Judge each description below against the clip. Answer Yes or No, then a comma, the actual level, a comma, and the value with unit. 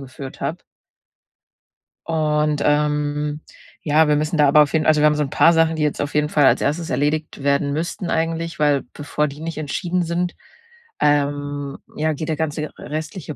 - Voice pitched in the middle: Yes, medium, 150 Hz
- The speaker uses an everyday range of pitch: No, narrow, 1.6 semitones